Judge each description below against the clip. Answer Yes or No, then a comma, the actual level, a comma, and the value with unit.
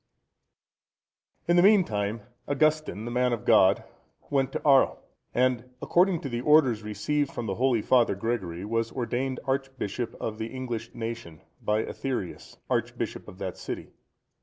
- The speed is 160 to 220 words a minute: No, average, 150 wpm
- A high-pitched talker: No, low, 120 Hz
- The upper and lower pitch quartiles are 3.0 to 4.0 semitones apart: Yes, average, 3.4 semitones